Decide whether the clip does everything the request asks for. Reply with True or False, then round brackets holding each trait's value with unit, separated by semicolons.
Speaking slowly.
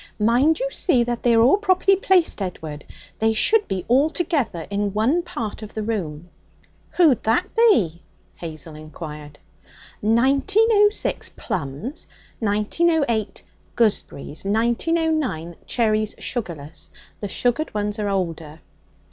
True (120 wpm)